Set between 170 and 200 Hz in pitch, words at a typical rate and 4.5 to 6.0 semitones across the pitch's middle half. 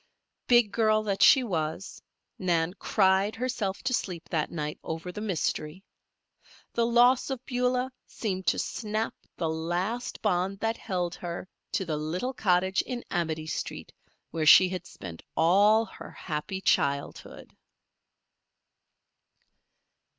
No: high, 190 Hz; slow, 130 wpm; average, 5.1 semitones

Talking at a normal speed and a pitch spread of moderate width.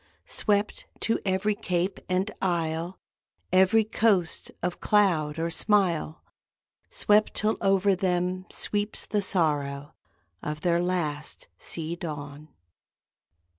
No: slow, 105 wpm; average, 3.9 semitones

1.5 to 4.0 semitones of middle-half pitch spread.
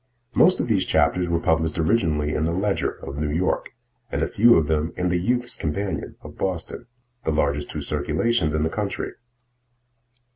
No: average, 4.4 semitones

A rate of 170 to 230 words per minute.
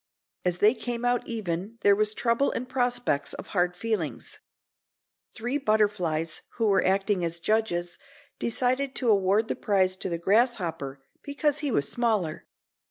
No: average, 150 wpm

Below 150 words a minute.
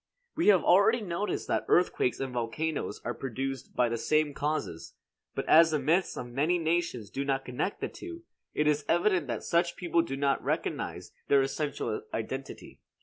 No: average, 175 wpm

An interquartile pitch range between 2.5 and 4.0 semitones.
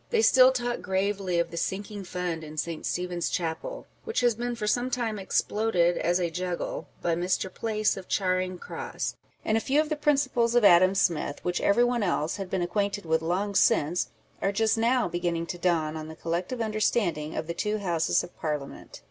No: average, 4.7 semitones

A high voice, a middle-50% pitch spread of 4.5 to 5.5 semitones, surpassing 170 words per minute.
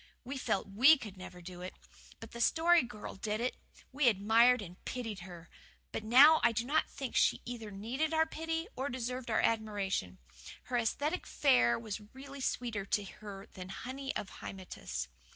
Yes: high, 230 Hz; average, 5.1 semitones; average, 180 wpm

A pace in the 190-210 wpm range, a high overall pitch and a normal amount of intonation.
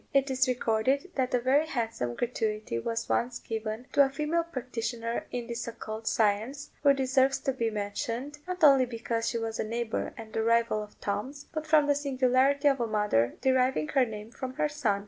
Yes: average, 195 wpm; high, 245 Hz; average, 3.6 semitones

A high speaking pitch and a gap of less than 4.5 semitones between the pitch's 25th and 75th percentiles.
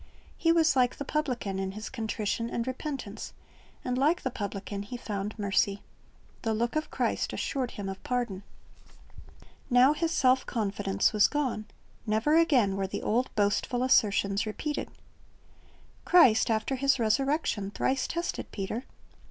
No: high, 235 Hz; average, 4.9 semitones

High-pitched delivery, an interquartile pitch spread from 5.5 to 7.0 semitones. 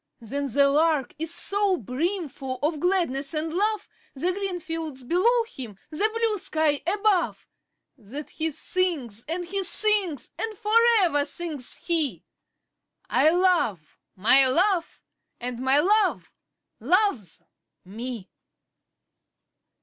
Yes: very high, 320 Hz; wide, 5.9 semitones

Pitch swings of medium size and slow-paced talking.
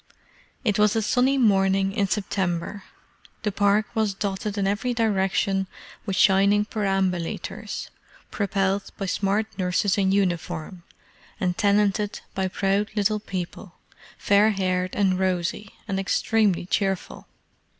No: narrow, 1.7 semitones; slow, 120 wpm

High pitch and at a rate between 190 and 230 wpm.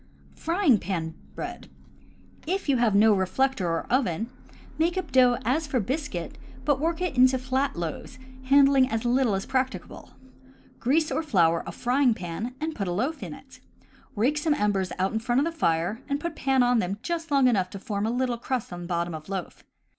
Yes: very high, 250 Hz; average, 200 wpm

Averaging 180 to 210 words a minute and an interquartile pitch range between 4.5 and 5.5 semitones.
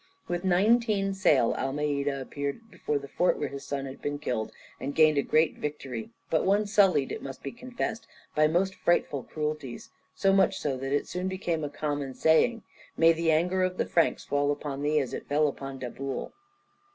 Yes: average, 190 wpm; average, 4.8 semitones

